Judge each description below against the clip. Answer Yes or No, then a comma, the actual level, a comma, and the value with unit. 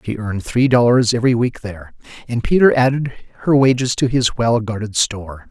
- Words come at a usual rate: Yes, average, 185 wpm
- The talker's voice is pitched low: Yes, low, 120 Hz